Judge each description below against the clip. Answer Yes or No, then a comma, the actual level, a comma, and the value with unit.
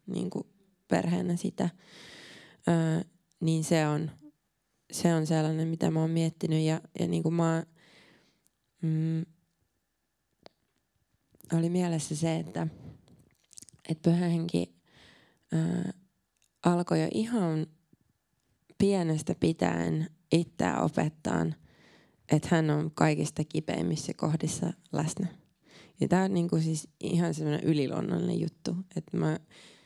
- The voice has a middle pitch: Yes, medium, 165 Hz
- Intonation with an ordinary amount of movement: No, narrow, 2.0 semitones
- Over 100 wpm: No, slow, 95 wpm